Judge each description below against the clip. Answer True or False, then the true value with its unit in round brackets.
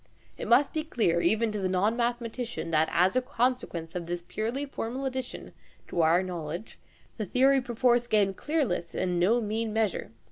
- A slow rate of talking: False (175 wpm)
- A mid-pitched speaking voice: False (220 Hz)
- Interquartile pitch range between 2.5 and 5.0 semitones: False (5.6 semitones)